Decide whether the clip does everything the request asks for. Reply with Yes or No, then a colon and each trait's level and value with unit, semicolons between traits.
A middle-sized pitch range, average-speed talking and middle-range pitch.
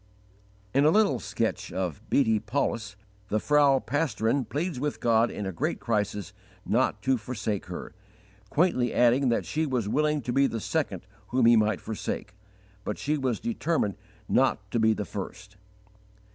No: average, 4.9 semitones; average, 160 wpm; low, 120 Hz